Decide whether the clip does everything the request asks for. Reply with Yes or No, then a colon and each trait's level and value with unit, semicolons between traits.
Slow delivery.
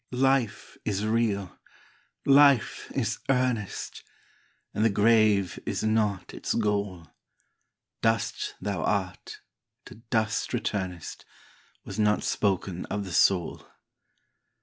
Yes: slow, 105 wpm